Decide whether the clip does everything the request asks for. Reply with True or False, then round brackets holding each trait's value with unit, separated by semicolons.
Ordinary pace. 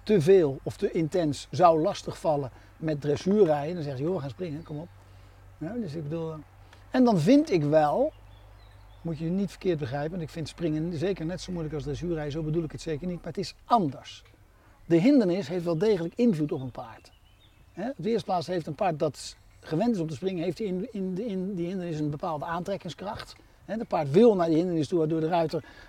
False (220 wpm)